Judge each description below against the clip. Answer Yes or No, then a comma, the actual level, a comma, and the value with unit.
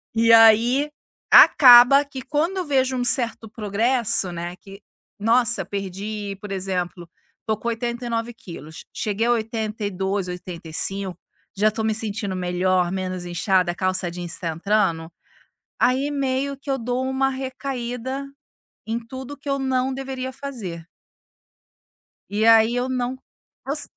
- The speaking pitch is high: Yes, high, 225 Hz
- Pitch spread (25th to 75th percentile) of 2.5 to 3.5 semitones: No, average, 5.3 semitones